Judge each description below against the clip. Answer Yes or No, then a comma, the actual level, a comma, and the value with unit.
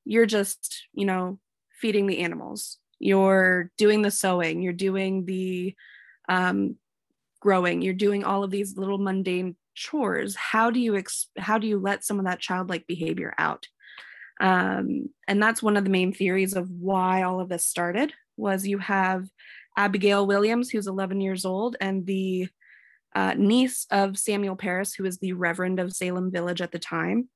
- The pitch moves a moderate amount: No, narrow, 1.9 semitones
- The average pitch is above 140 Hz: Yes, high, 190 Hz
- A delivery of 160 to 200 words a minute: Yes, average, 170 wpm